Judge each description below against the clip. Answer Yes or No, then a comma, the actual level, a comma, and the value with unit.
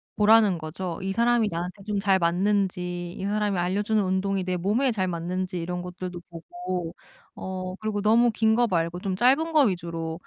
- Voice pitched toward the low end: No, high, 190 Hz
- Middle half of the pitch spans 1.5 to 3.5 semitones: Yes, average, 3.1 semitones